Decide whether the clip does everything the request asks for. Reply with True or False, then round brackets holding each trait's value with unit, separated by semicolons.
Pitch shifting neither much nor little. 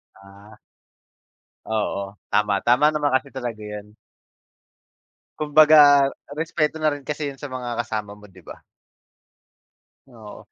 False (5.9 semitones)